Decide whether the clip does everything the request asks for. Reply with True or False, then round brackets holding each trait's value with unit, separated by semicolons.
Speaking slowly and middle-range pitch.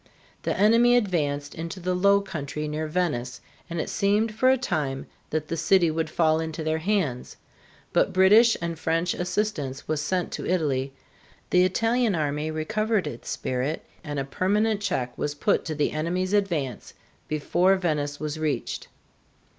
False (160 wpm; 165 Hz)